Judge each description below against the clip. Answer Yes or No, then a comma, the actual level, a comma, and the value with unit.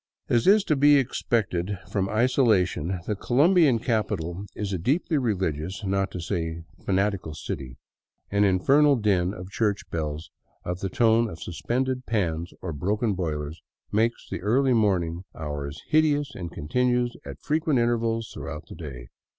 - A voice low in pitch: Yes, low, 100 Hz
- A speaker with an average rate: Yes, average, 155 wpm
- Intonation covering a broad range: Yes, wide, 6.0 semitones